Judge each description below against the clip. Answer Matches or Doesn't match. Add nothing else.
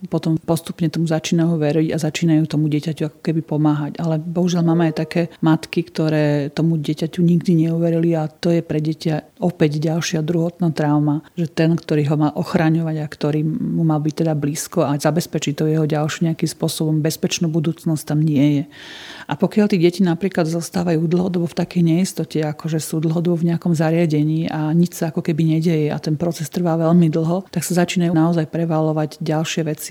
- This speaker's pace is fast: Matches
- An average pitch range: Doesn't match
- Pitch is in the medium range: Matches